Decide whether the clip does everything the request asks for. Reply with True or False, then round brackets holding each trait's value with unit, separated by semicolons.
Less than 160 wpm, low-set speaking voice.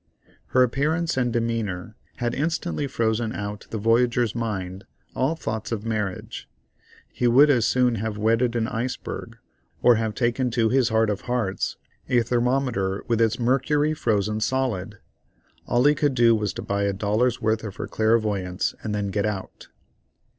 False (165 wpm; 115 Hz)